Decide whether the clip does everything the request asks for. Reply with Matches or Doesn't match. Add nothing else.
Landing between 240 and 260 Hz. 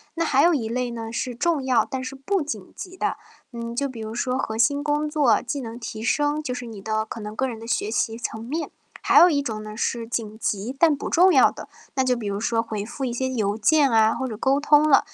Matches